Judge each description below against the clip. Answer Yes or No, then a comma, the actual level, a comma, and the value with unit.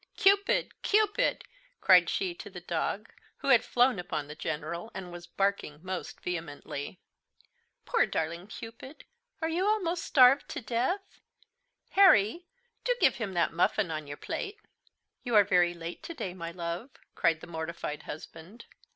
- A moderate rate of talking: Yes, average, 150 wpm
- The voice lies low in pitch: No, high, 195 Hz